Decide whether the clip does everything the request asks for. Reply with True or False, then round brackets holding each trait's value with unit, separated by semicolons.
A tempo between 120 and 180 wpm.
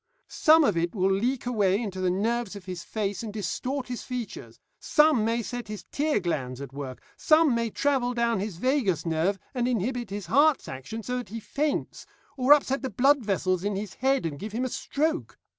False (205 wpm)